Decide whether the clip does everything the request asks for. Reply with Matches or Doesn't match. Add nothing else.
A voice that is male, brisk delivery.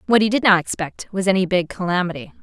Doesn't match